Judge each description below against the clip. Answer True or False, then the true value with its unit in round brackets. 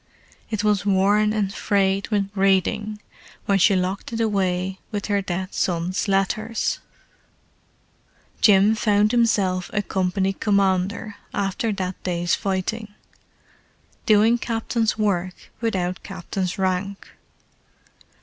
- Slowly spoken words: True (105 wpm)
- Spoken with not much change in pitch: True (2.1 semitones)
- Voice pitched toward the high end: True (200 Hz)